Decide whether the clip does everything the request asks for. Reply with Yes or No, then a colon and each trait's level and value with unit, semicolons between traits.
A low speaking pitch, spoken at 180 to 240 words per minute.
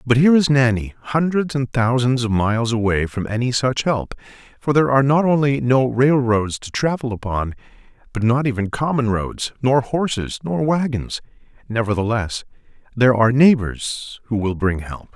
No: low, 125 Hz; average, 160 wpm